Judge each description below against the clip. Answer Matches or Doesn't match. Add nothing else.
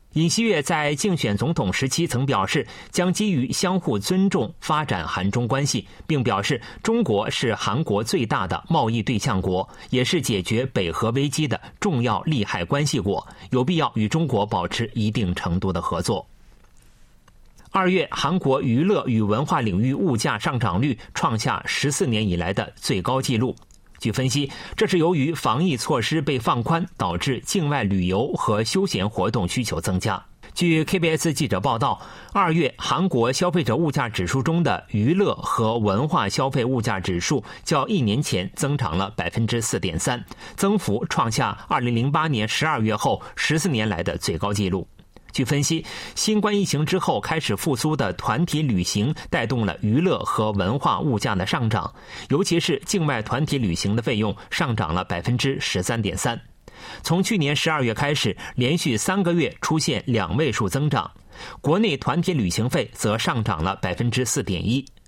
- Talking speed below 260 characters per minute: Doesn't match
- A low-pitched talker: Matches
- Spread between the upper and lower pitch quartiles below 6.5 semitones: Doesn't match